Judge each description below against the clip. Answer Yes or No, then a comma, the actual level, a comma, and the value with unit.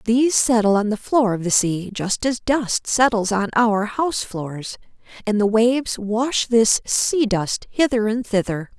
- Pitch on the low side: No, high, 220 Hz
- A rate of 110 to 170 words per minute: No, average, 180 wpm